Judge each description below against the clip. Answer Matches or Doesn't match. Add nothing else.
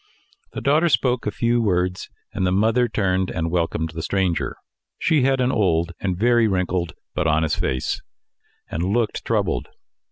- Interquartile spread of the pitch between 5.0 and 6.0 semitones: Matches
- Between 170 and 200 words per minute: Doesn't match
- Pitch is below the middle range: Matches